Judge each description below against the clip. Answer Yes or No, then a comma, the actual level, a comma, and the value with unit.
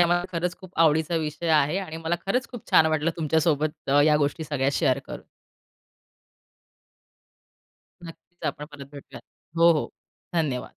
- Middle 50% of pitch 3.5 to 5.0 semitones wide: No, narrow, 2.4 semitones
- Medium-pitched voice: Yes, medium, 160 Hz